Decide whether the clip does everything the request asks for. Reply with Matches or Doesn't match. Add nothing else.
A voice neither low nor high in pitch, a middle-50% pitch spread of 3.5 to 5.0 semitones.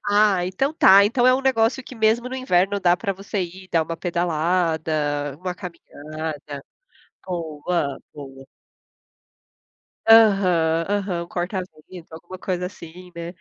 Matches